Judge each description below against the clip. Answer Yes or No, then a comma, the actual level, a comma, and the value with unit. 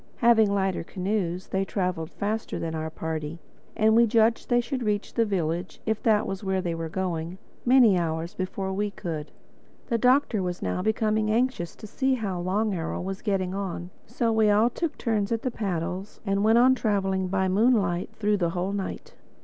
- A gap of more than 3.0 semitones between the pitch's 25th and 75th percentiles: Yes, average, 3.5 semitones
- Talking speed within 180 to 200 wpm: Yes, average, 185 wpm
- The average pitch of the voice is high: Yes, high, 195 Hz